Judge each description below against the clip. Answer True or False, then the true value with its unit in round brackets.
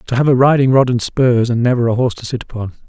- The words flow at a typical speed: False (290 wpm)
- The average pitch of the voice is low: True (125 Hz)